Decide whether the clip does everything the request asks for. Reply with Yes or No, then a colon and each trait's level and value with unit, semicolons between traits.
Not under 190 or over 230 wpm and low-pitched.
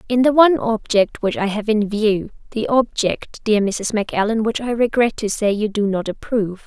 No: average, 200 wpm; high, 215 Hz